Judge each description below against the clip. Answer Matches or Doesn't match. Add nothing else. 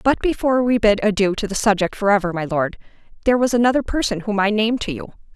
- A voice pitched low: Doesn't match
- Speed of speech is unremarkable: Doesn't match